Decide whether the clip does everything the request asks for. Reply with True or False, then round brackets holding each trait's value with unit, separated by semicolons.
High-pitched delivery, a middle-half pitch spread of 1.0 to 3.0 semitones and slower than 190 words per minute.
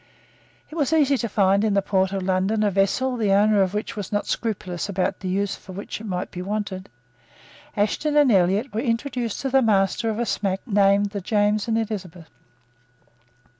False (205 Hz; 2.7 semitones; 195 wpm)